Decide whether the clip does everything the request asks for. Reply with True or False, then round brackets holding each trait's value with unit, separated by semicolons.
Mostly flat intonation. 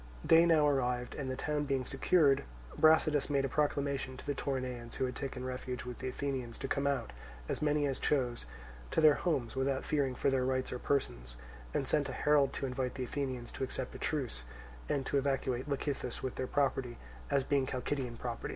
True (2.0 semitones)